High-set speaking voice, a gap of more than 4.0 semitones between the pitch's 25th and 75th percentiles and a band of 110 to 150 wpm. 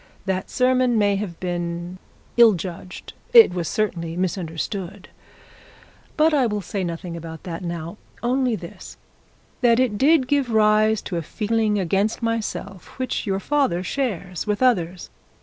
Yes: high, 200 Hz; average, 5.0 semitones; average, 145 wpm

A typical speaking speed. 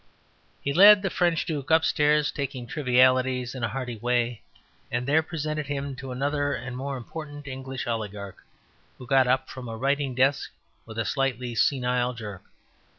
Yes: average, 160 wpm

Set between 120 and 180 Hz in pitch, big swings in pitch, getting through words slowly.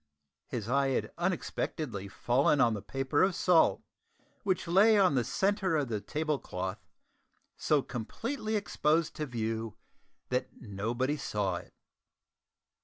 Yes: low, 135 Hz; wide, 7.1 semitones; slow, 130 wpm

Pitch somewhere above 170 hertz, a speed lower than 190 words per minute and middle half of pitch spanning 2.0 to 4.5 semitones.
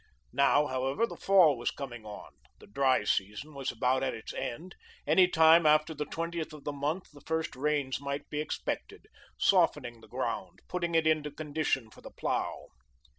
No: medium, 145 Hz; average, 175 wpm; average, 3.4 semitones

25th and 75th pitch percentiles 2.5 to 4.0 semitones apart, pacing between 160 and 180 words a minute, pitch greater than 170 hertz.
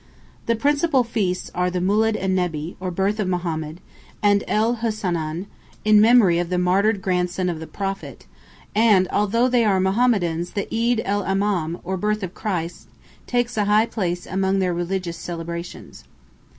Yes: average, 3.3 semitones; average, 165 wpm; high, 190 Hz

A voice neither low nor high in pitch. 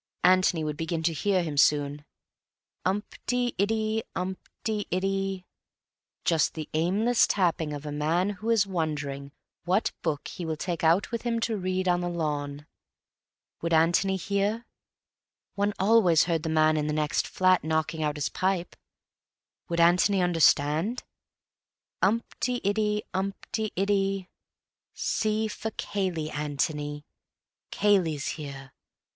Yes: medium, 180 Hz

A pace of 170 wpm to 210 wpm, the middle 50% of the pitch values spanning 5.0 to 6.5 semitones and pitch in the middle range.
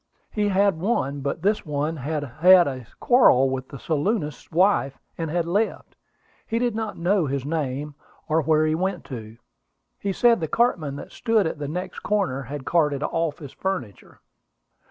Yes: average, 175 wpm; wide, 5.4 semitones; medium, 160 Hz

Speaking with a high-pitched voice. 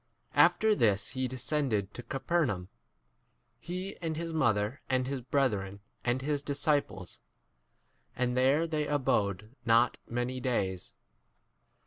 No: low, 130 Hz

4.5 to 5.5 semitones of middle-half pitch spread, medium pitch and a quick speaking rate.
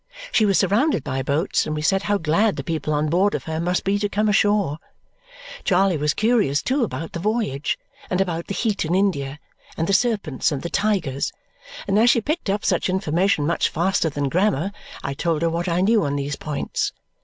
Yes: average, 5.0 semitones; medium, 180 Hz; fast, 210 wpm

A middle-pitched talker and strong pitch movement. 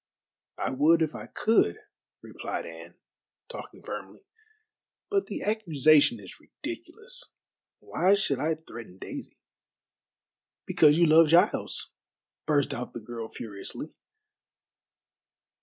Yes: medium, 150 Hz; wide, 6.7 semitones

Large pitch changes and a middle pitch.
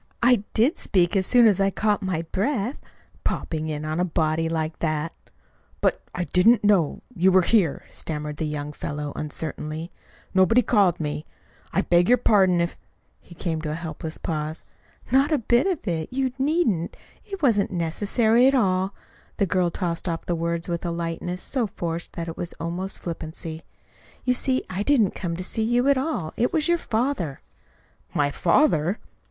Yes: wide, 5.7 semitones; medium, 180 Hz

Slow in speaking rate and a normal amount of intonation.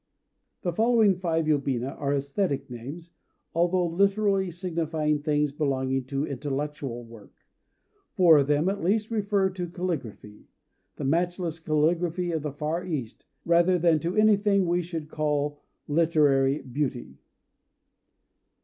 Yes: slow, 130 wpm; average, 4.0 semitones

